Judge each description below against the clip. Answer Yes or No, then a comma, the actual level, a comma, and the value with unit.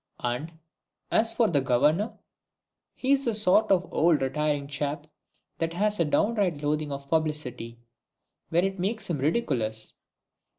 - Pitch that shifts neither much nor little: No, wide, 6.0 semitones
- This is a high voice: No, medium, 160 Hz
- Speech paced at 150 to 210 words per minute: No, slow, 135 wpm